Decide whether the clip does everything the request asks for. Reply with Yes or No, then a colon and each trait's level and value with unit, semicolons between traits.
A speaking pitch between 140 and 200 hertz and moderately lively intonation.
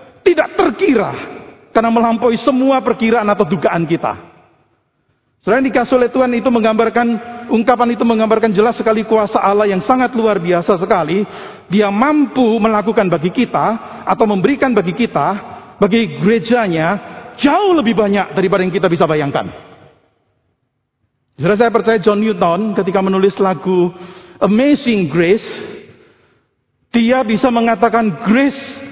No: high, 220 Hz; average, 4.0 semitones